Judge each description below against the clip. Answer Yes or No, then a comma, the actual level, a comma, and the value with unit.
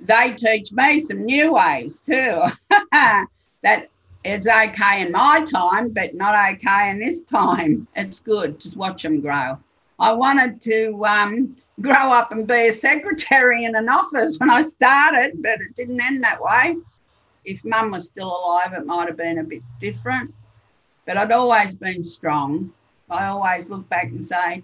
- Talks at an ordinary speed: Yes, average, 170 wpm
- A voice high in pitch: Yes, high, 215 Hz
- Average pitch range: No, wide, 6.1 semitones